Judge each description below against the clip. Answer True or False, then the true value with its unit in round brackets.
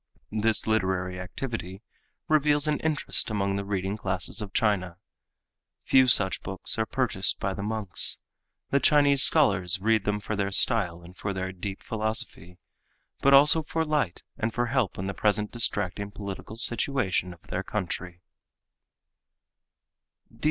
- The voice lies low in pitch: True (105 Hz)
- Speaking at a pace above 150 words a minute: False (145 wpm)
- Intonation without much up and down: False (4.2 semitones)